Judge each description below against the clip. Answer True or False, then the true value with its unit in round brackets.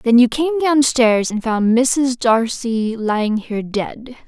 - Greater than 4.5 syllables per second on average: False (3.6 syllables/s)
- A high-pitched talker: True (240 Hz)